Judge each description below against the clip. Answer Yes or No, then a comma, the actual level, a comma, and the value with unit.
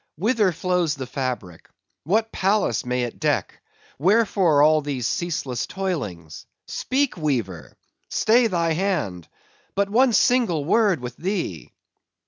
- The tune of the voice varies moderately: No, wide, 8.1 semitones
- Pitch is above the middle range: No, medium, 165 Hz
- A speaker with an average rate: No, slow, 110 wpm